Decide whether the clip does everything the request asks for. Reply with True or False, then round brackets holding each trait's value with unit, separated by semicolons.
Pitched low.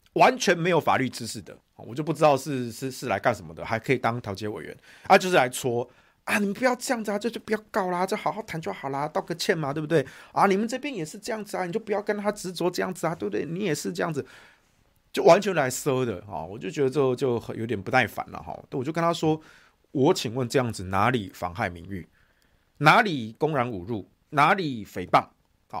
False (155 Hz)